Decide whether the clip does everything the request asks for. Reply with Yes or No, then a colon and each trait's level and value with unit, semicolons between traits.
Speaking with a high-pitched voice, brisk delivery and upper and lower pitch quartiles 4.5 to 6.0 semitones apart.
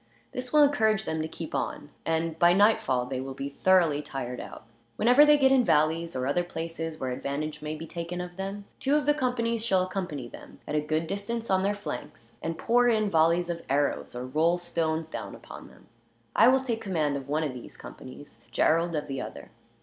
No: medium, 165 Hz; fast, 210 wpm; wide, 5.6 semitones